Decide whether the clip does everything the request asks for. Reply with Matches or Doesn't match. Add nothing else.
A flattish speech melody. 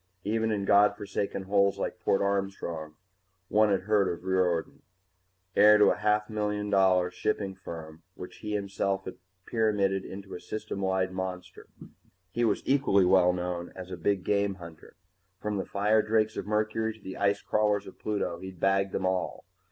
Matches